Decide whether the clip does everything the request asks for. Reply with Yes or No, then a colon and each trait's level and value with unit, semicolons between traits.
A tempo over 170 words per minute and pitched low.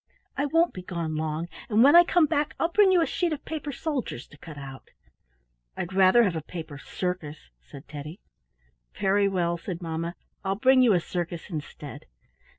No: average, 185 wpm; medium, 180 Hz